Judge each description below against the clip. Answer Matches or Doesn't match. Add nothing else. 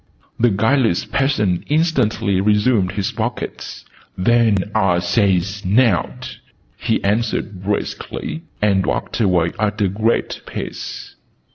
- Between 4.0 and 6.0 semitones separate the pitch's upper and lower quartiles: Doesn't match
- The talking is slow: Matches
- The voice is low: Matches